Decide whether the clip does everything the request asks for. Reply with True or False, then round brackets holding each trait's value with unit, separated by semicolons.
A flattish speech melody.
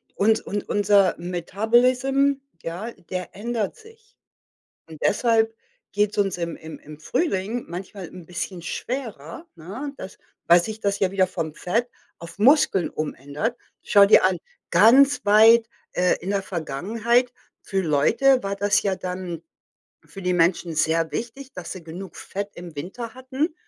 False (4.9 semitones)